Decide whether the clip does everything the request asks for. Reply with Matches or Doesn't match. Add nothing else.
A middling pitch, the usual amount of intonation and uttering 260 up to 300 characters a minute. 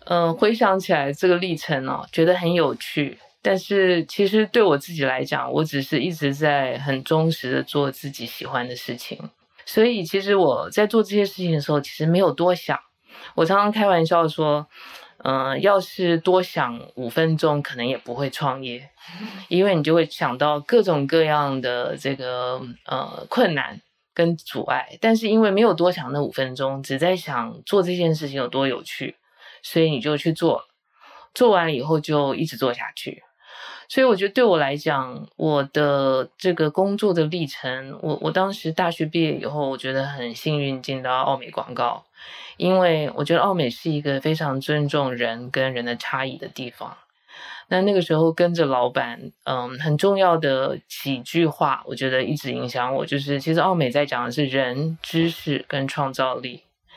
Matches